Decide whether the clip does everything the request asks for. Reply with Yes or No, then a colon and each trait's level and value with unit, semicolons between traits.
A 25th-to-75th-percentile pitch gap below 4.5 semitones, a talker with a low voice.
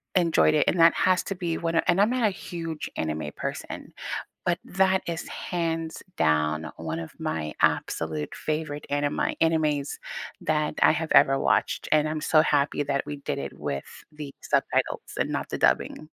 No: average, 3.2 semitones; medium, 155 Hz